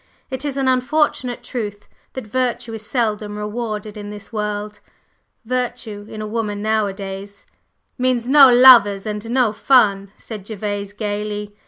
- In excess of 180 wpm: No, average, 145 wpm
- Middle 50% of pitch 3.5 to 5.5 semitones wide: No, average, 3.0 semitones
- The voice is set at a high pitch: Yes, high, 215 Hz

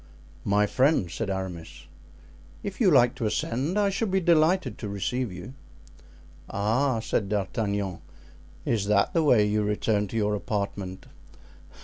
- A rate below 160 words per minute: Yes, average, 140 wpm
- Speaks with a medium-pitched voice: No, low, 105 Hz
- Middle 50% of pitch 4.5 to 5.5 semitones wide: Yes, average, 5.1 semitones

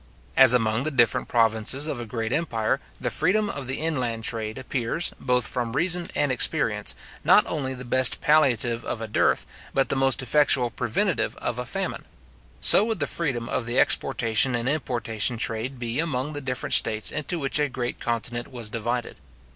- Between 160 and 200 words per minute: Yes, average, 180 wpm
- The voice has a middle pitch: No, low, 125 Hz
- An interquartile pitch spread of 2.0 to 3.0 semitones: No, average, 3.7 semitones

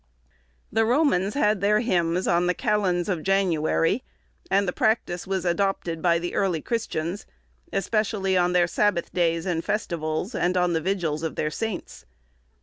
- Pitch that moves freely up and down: No, average, 3.2 semitones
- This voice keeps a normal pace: Yes, average, 155 wpm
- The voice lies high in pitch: No, medium, 180 Hz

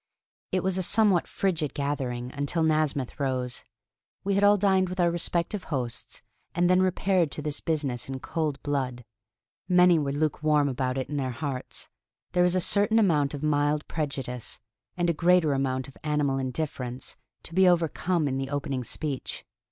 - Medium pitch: Yes, medium, 150 Hz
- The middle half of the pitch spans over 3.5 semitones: Yes, average, 4.7 semitones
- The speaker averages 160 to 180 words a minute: Yes, average, 170 wpm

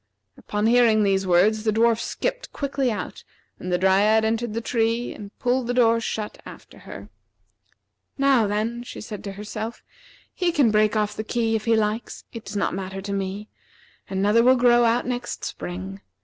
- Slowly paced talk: No, average, 180 wpm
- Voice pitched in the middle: No, high, 220 Hz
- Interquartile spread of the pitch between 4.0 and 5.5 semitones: No, average, 2.7 semitones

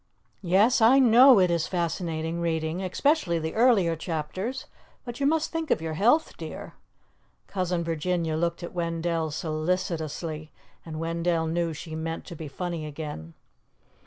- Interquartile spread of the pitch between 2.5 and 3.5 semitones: Yes, average, 3.0 semitones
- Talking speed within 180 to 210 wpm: No, average, 145 wpm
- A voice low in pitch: No, medium, 170 Hz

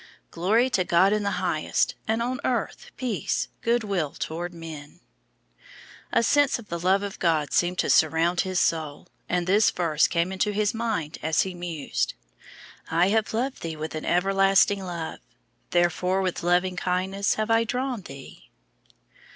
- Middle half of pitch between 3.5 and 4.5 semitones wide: Yes, average, 3.8 semitones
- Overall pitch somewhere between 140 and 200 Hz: Yes, medium, 185 Hz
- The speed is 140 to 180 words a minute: Yes, average, 160 wpm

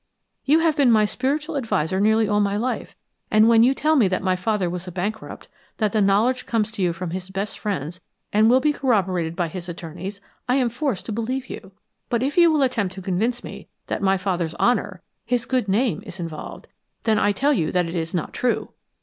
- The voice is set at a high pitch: Yes, high, 210 Hz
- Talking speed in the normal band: No, fast, 220 wpm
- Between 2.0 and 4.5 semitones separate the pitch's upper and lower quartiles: No, average, 5.2 semitones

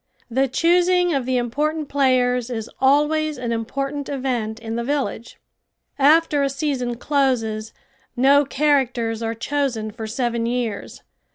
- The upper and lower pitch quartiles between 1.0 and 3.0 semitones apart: No, average, 3.6 semitones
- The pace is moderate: No, slow, 130 wpm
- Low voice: No, very high, 260 Hz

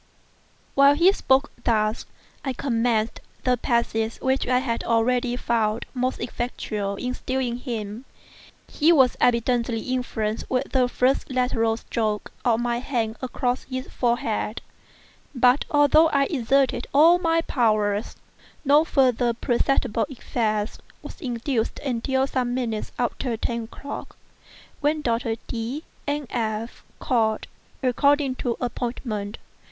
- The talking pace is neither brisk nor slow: No, slow, 125 wpm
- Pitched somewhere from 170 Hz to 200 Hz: No, high, 245 Hz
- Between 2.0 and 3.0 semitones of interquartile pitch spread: Yes, average, 2.7 semitones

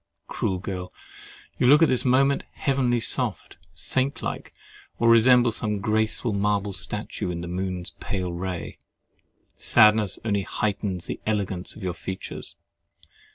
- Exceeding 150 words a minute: No, slow, 135 wpm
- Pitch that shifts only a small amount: No, average, 4.1 semitones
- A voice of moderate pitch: No, low, 105 Hz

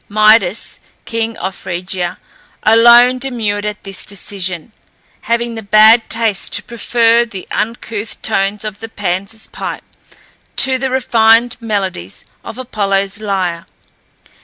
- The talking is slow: Yes, slow, 120 wpm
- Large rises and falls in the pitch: No, average, 2.9 semitones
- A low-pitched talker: No, high, 215 Hz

